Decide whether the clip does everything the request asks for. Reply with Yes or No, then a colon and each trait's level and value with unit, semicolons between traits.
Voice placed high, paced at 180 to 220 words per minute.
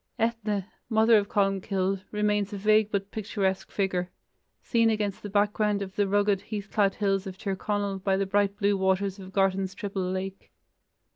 No: high, 200 Hz; average, 170 wpm